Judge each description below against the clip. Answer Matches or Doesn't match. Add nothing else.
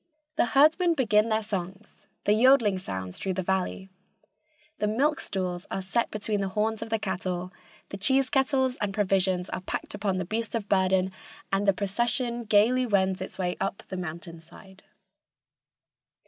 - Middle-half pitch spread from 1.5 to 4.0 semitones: Matches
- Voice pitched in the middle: Doesn't match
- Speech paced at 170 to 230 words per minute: Doesn't match